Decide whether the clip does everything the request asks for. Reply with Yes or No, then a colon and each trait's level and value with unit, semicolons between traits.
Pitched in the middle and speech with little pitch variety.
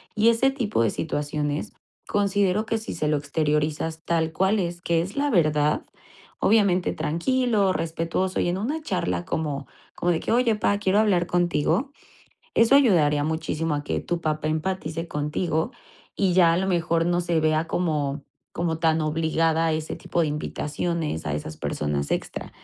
No: medium, 165 Hz; average, 3.8 semitones